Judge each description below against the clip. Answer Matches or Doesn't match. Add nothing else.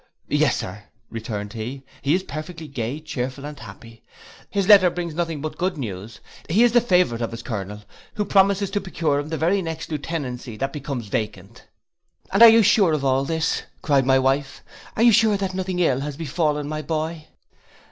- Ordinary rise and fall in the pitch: Doesn't match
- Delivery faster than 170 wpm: Matches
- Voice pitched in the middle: Matches